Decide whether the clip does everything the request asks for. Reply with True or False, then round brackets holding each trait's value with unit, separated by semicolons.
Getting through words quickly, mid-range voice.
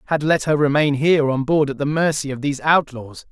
True (235 wpm; 145 Hz)